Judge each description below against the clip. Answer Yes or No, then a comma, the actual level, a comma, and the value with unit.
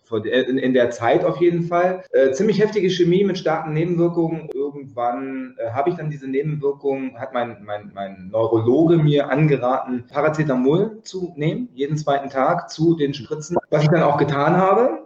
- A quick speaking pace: No, average, 165 wpm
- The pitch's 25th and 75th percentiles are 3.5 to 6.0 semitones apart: Yes, average, 4.6 semitones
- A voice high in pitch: No, medium, 145 Hz